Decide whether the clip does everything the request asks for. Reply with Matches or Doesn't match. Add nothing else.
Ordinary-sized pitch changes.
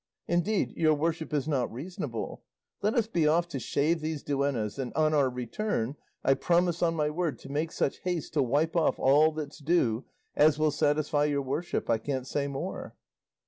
Matches